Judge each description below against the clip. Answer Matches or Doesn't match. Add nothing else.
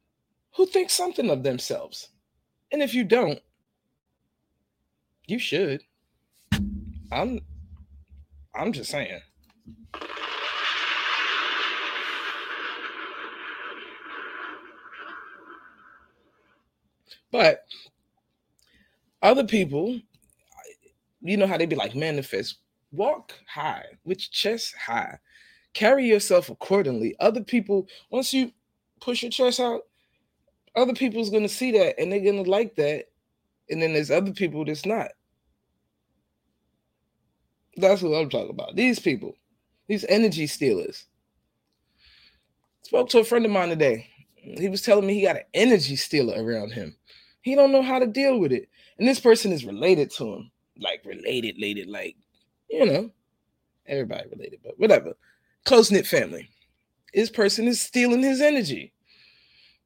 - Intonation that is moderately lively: Doesn't match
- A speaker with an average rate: Doesn't match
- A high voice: Matches